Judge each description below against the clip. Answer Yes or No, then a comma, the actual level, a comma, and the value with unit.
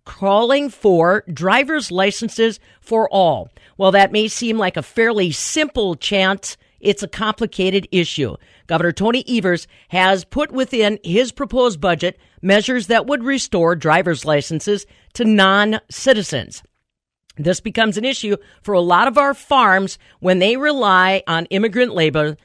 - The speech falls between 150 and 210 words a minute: No, average, 140 wpm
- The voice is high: Yes, high, 200 Hz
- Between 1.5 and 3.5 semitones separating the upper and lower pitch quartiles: No, average, 4.4 semitones